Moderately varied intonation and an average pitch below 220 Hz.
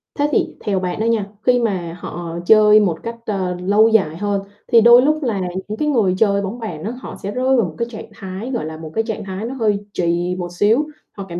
Yes: average, 4.1 semitones; high, 205 Hz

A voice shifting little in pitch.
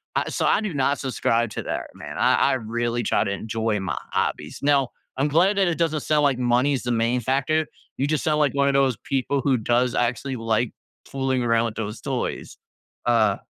No: average, 3.3 semitones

